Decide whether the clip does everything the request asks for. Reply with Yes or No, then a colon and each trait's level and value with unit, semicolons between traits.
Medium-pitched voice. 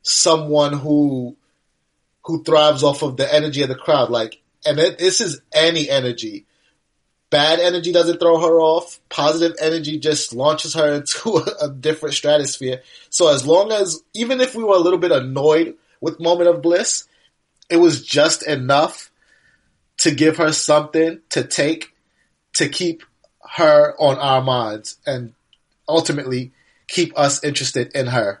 Yes: medium, 155 Hz